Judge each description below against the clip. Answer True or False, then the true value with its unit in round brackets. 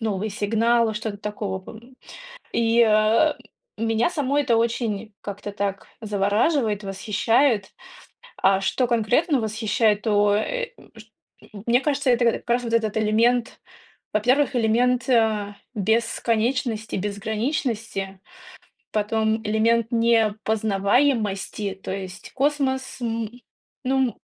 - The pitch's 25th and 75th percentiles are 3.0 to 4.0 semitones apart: False (2.6 semitones)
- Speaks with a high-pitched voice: True (225 Hz)